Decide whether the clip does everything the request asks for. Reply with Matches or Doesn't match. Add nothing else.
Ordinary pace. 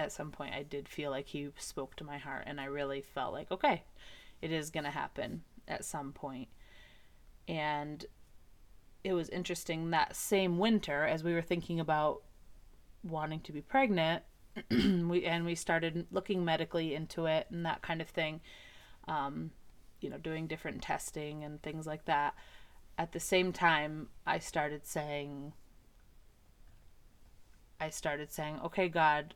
Matches